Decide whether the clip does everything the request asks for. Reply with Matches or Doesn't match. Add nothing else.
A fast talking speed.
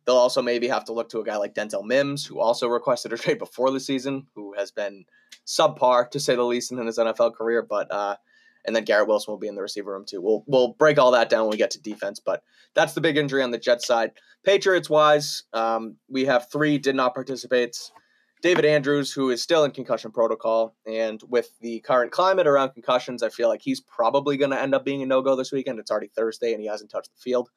Matches